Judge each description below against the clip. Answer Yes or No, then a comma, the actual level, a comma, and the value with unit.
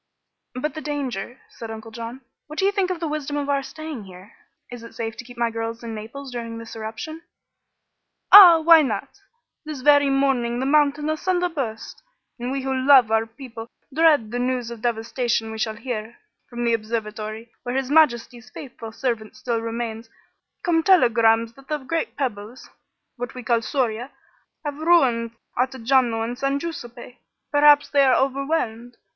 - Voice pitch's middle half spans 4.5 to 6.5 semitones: No, average, 4.0 semitones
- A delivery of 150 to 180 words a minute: Yes, average, 170 wpm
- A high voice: Yes, high, 245 Hz